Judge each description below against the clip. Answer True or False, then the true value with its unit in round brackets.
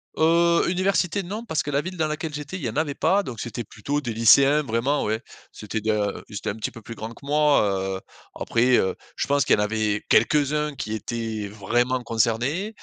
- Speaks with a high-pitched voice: False (130 Hz)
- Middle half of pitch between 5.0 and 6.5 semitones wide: True (5.5 semitones)